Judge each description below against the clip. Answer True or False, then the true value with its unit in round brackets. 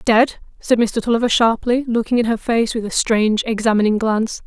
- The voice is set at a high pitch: True (225 Hz)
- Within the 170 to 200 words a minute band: True (190 wpm)